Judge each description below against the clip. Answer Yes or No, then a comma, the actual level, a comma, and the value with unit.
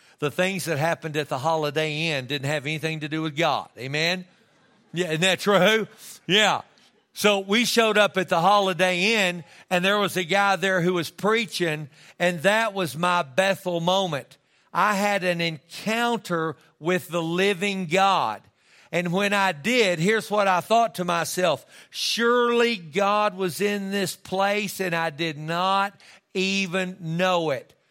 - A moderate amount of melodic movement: Yes, average, 3.3 semitones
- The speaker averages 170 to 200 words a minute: No, average, 160 wpm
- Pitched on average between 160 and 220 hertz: Yes, medium, 185 Hz